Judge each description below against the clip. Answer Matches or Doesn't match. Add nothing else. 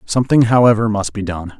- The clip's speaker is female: Doesn't match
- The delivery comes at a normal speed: Matches